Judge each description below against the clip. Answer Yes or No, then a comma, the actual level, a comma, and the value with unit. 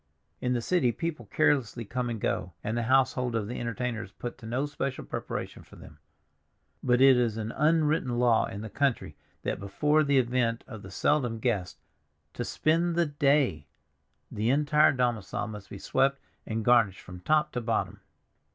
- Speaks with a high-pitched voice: No, low, 120 Hz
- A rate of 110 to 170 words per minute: No, average, 180 wpm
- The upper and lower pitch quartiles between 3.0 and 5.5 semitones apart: Yes, average, 3.8 semitones